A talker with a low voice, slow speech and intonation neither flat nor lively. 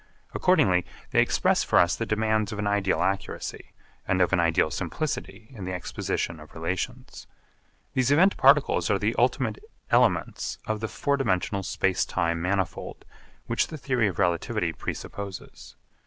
No: low, 100 Hz; average, 155 wpm; average, 4.5 semitones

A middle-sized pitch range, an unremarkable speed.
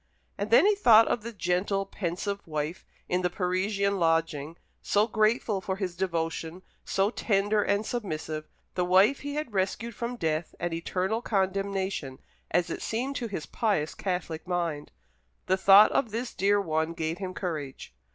Yes: average, 4.0 semitones; average, 160 wpm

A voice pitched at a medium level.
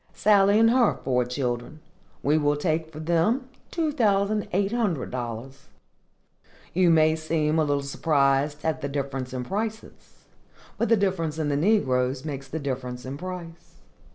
Yes: medium, 155 Hz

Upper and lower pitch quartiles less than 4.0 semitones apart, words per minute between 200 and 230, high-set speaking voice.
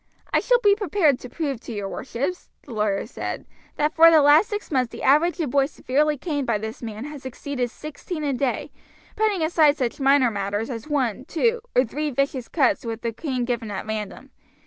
No: average, 4.6 semitones; fast, 205 wpm; very high, 275 Hz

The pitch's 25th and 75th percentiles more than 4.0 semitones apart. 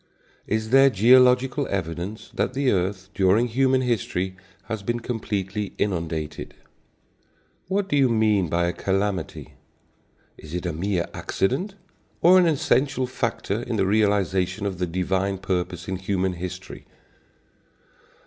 Yes: average, 5.0 semitones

